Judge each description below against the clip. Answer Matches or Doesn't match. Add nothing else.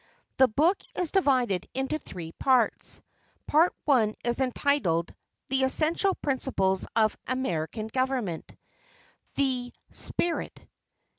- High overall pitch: Matches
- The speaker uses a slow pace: Matches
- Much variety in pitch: Doesn't match